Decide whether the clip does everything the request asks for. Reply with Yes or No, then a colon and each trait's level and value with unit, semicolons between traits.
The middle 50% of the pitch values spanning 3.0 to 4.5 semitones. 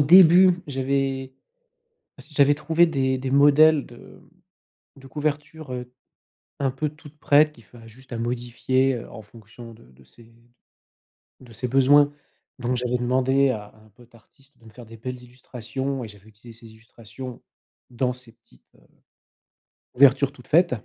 Yes: average, 3.3 semitones